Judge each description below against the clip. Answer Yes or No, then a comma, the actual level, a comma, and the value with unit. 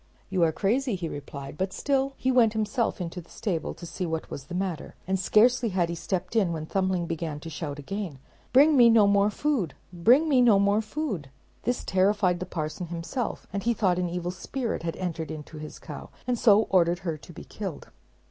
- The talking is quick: Yes, fast, 215 wpm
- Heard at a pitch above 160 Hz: Yes, medium, 185 Hz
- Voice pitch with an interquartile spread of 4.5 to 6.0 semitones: Yes, average, 4.8 semitones